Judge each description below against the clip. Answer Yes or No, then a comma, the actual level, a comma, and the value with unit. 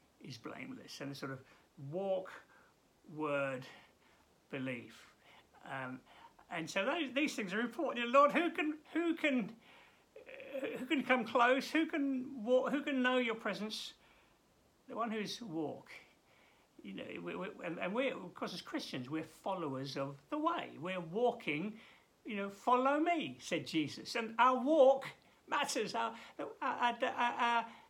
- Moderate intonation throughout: No, wide, 8.3 semitones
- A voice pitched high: Yes, high, 235 Hz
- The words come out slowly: No, average, 160 wpm